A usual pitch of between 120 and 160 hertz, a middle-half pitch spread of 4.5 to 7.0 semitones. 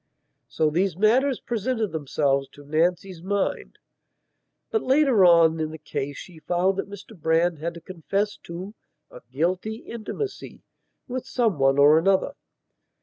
No: medium, 180 Hz; average, 5.1 semitones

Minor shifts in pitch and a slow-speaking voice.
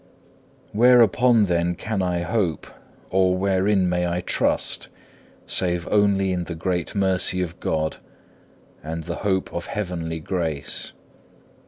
Yes: narrow, 2.3 semitones; slow, 125 wpm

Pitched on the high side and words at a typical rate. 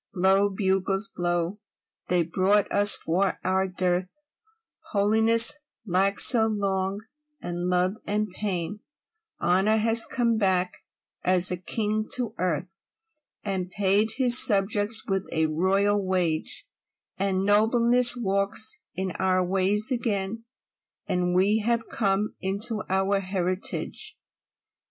No: high, 195 Hz; slow, 115 wpm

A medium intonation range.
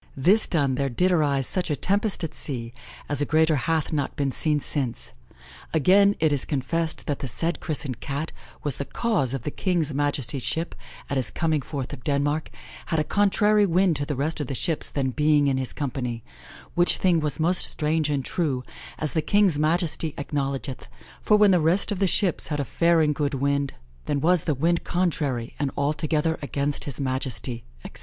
Yes: average, 3.3 semitones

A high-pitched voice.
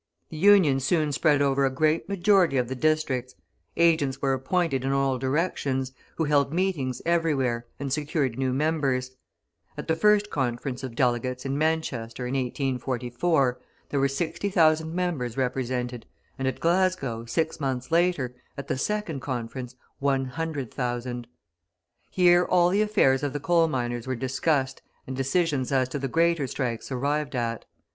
No: low, 135 Hz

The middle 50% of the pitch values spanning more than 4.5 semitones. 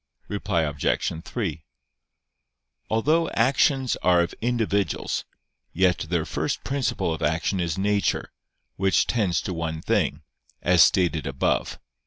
Yes: wide, 5.5 semitones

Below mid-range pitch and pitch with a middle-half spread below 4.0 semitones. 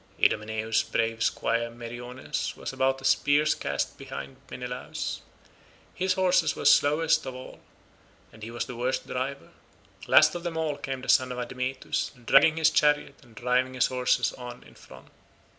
Yes: low, 130 Hz; average, 3.2 semitones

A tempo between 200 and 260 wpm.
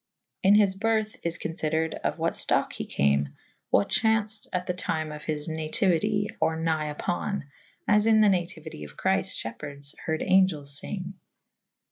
No: average, 165 wpm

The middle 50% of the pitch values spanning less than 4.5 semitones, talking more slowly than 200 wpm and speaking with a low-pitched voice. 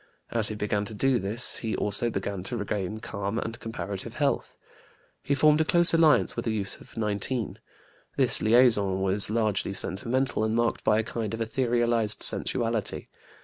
Yes: narrow, 2.6 semitones; average, 170 wpm; low, 110 Hz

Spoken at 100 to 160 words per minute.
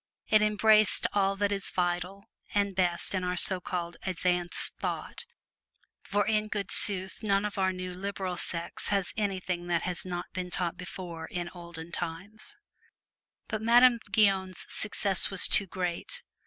Yes: average, 155 wpm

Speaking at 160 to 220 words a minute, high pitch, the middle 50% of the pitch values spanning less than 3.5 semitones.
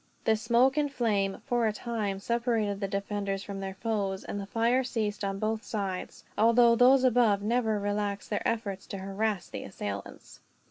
Yes: average, 175 wpm; high, 210 Hz; average, 2.9 semitones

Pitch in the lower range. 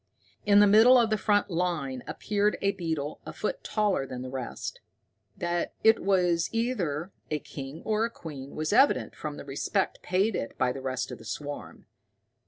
No: medium, 175 Hz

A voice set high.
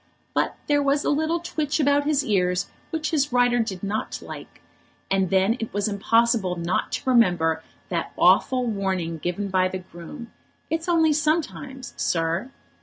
Yes: high, 230 Hz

